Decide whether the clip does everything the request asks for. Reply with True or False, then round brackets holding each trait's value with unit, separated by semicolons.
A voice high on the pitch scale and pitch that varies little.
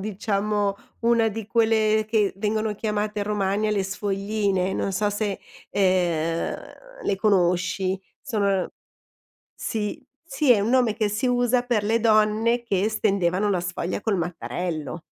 True (210 Hz; 2.3 semitones)